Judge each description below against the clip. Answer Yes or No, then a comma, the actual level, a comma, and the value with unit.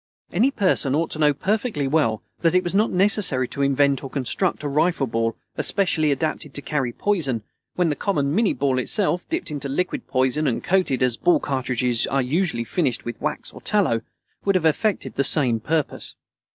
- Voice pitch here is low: No, medium, 150 Hz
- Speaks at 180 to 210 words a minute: Yes, average, 190 wpm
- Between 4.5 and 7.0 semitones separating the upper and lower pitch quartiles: Yes, wide, 5.6 semitones